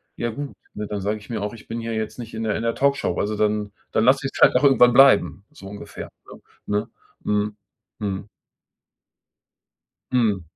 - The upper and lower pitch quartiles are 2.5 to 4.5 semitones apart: Yes, average, 2.9 semitones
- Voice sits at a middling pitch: No, low, 110 Hz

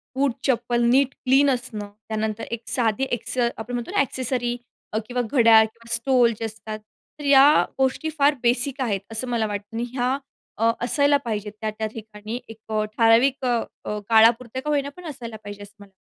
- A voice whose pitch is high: Yes, high, 235 Hz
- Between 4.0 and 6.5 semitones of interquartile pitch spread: No, average, 3.0 semitones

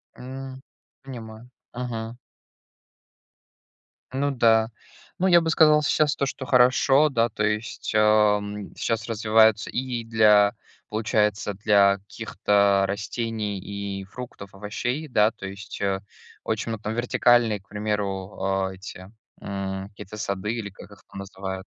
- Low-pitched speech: Yes, low, 105 Hz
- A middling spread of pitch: Yes, average, 3.2 semitones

